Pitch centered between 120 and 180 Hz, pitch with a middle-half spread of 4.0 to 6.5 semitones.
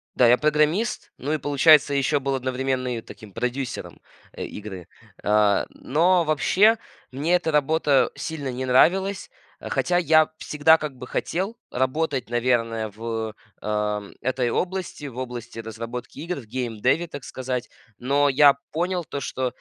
Yes: low, 135 Hz; average, 4.5 semitones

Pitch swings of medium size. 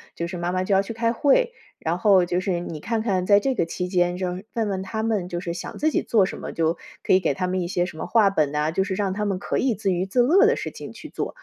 Yes: average, 3.7 semitones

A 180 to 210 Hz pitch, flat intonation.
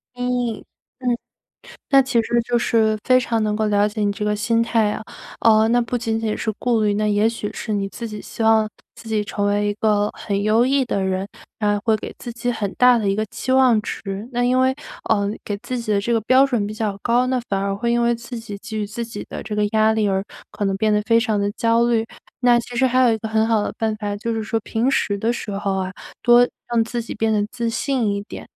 No: high, 220 Hz; narrow, 2.3 semitones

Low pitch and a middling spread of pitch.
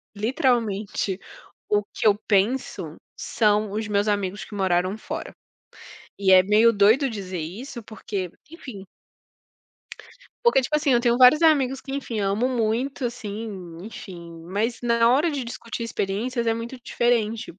No: high, 220 Hz; average, 3.7 semitones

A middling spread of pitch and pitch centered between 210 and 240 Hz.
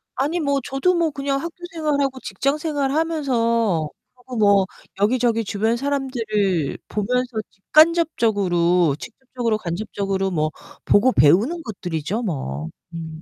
No: wide, 6.5 semitones; high, 230 Hz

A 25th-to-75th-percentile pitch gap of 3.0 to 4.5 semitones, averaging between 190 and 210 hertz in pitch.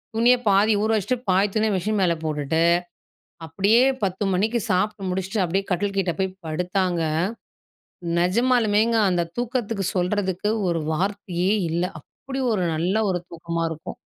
Yes: average, 3.4 semitones; high, 195 Hz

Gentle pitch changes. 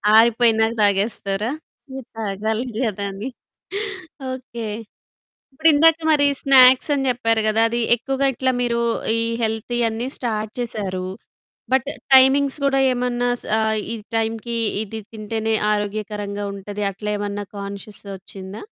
No: average, 3.3 semitones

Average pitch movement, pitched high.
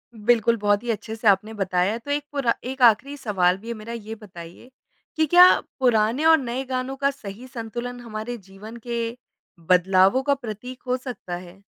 Yes: average, 3.7 semitones; high, 230 Hz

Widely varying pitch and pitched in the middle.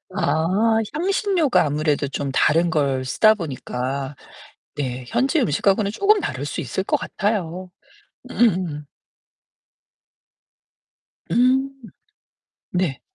Yes: wide, 8.0 semitones; medium, 175 Hz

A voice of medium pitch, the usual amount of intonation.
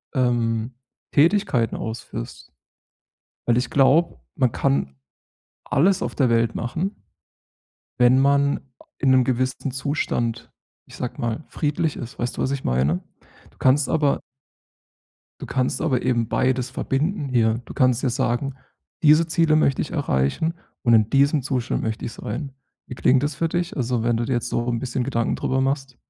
No: low, 130 Hz; average, 3.2 semitones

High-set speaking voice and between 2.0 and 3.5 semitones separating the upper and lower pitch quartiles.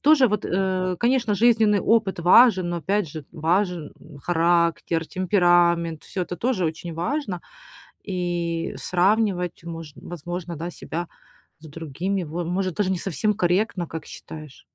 No: medium, 175 Hz; average, 2.9 semitones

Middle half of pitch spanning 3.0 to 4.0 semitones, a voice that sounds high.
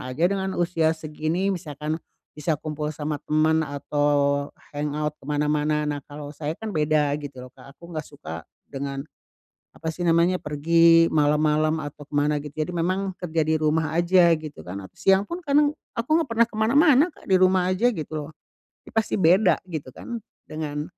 No: average, 3.3 semitones; medium, 155 Hz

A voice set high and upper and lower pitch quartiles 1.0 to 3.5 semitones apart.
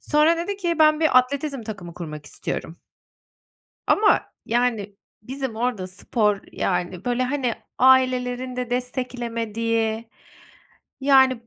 Yes: very high, 250 Hz; average, 3.2 semitones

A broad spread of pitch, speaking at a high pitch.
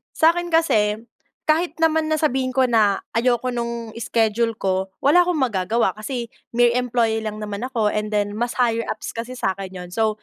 No: average, 3.3 semitones; high, 235 Hz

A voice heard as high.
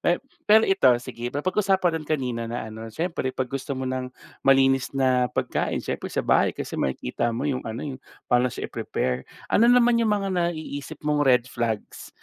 No: low, 135 Hz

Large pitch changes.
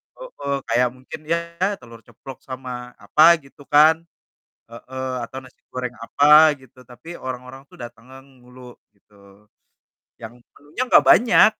No: average, 3.5 semitones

